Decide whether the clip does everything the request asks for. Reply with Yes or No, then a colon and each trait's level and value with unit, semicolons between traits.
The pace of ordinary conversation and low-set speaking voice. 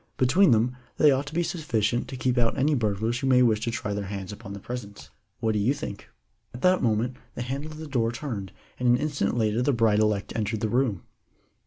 No: fast, 230 wpm; low, 120 Hz